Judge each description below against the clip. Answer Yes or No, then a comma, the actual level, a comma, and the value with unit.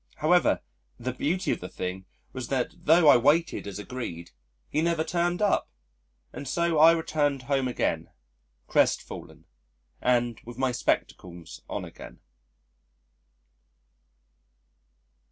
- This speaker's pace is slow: Yes, slow, 120 wpm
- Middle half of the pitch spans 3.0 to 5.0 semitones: No, wide, 5.6 semitones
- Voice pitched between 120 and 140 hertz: Yes, low, 135 Hz